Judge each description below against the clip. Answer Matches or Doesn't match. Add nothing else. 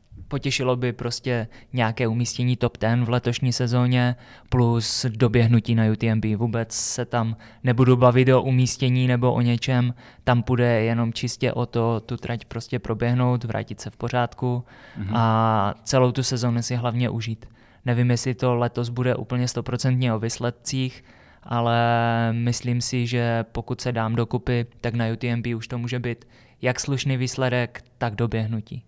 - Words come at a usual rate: Matches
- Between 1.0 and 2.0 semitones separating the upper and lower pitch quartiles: Matches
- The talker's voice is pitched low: Matches